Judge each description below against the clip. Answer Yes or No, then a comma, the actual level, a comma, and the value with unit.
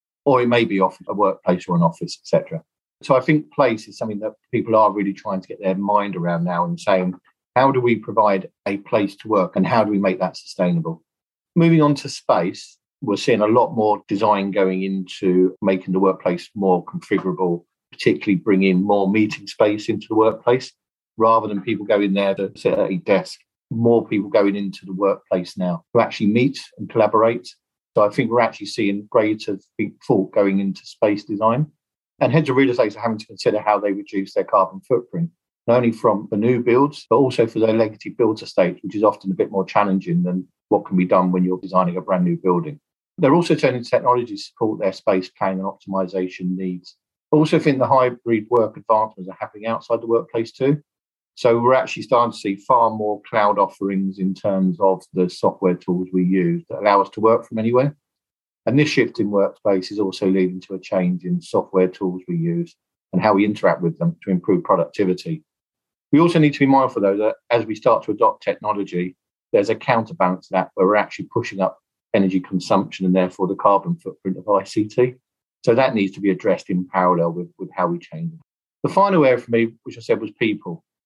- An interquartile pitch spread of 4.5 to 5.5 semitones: Yes, average, 5.0 semitones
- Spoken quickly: Yes, fast, 210 wpm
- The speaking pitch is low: Yes, low, 100 Hz